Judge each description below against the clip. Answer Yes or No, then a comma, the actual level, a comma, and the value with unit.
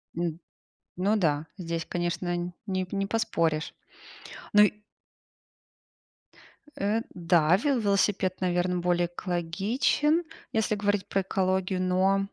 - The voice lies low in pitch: No, medium, 185 Hz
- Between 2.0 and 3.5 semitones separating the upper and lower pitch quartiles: Yes, narrow, 2.6 semitones